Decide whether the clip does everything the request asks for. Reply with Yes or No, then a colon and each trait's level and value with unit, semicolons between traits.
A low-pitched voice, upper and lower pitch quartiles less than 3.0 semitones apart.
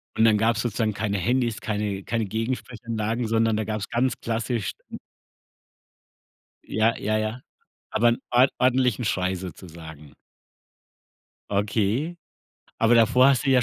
Yes: low, 110 Hz; narrow, 2.6 semitones